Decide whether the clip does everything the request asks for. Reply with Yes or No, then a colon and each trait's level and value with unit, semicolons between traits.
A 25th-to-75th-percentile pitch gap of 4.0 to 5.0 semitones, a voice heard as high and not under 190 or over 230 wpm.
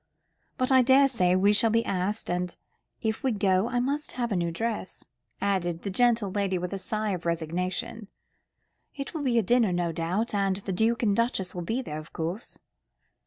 Yes: average, 4.5 semitones; high, 200 Hz; average, 195 wpm